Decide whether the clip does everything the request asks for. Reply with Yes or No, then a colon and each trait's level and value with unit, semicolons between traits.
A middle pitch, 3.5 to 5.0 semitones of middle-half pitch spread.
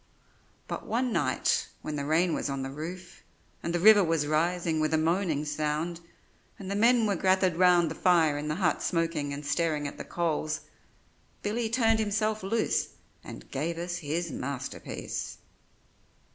Yes: medium, 170 Hz; average, 3.8 semitones